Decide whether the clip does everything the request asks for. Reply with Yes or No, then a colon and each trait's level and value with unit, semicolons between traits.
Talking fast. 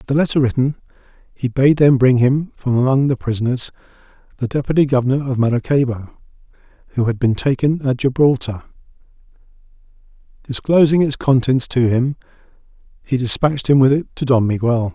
No: average, 145 wpm